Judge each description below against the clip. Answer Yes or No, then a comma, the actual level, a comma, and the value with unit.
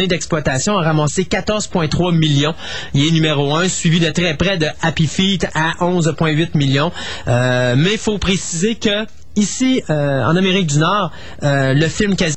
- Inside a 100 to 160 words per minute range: No, average, 170 wpm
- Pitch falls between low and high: Yes, medium, 165 Hz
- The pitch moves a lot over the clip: No, average, 4.0 semitones